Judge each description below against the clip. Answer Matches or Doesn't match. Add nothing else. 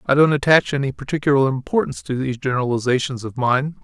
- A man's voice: Matches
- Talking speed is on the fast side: Doesn't match